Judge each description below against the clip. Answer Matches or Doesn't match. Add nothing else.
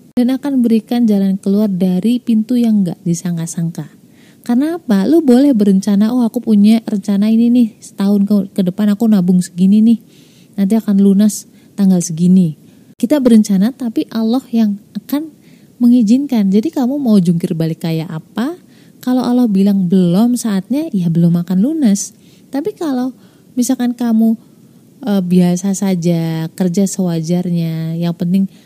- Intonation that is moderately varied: Matches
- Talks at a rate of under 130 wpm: Doesn't match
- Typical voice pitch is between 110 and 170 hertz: Doesn't match